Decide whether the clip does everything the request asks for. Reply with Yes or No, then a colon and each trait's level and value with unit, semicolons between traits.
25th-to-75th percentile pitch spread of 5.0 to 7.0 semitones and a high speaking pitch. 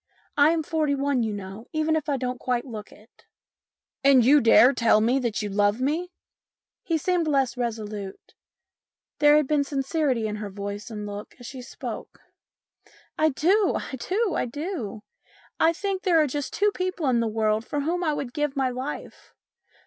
Yes: wide, 5.6 semitones; very high, 270 Hz